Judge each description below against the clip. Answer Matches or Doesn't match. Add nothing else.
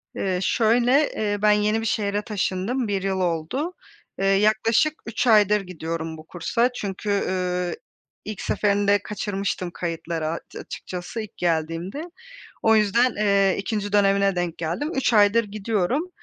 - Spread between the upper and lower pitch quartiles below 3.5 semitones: Matches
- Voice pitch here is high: Matches